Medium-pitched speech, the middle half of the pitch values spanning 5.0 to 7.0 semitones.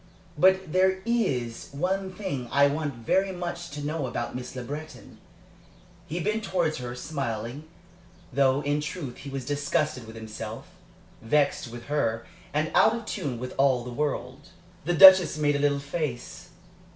Yes: medium, 145 Hz; wide, 5.6 semitones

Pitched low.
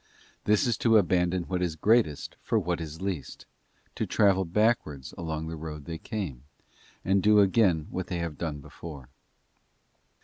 Yes: very low, 90 Hz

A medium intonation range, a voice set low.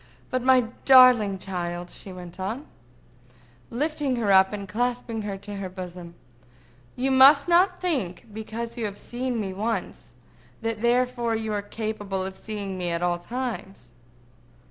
No: average, 4.6 semitones; high, 215 Hz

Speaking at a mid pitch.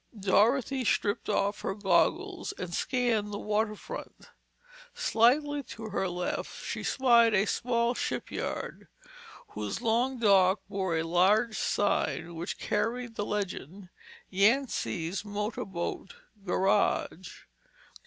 No: high, 210 Hz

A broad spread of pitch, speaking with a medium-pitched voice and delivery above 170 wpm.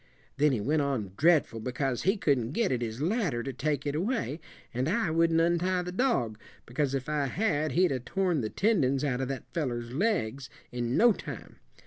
Yes: wide, 5.7 semitones; medium, 145 Hz; average, 195 wpm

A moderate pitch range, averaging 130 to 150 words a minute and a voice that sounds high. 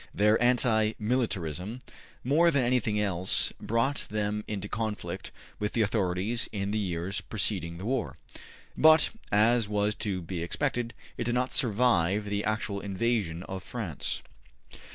No: average, 3.7 semitones; average, 140 wpm; low, 105 Hz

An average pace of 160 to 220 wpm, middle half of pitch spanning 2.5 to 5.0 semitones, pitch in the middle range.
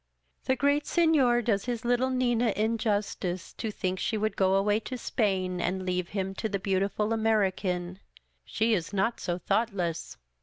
No: average, 165 wpm; average, 3.8 semitones; high, 210 Hz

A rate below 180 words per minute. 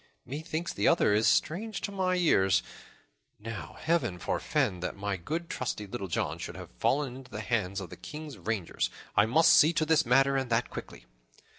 No: average, 185 wpm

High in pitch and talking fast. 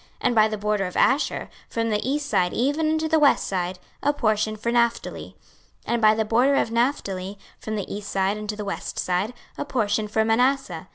Yes: high, 220 Hz; fast, 215 wpm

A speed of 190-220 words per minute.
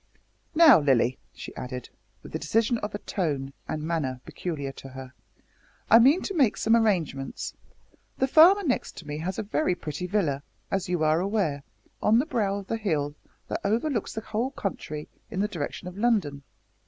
No: average, 180 wpm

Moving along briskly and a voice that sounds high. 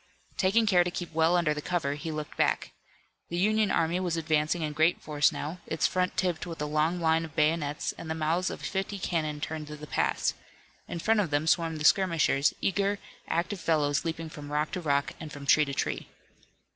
No: fast, 210 wpm; medium, 160 Hz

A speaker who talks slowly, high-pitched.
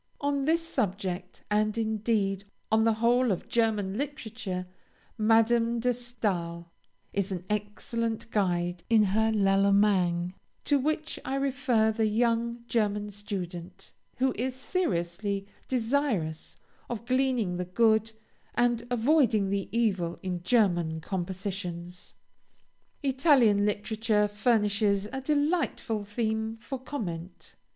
Yes: slow, 110 wpm; high, 215 Hz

